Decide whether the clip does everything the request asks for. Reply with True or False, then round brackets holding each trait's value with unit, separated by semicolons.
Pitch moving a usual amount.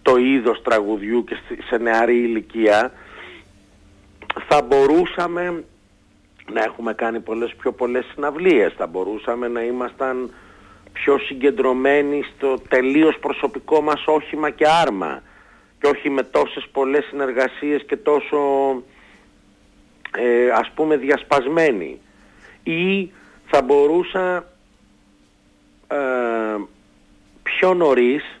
False (5.9 semitones)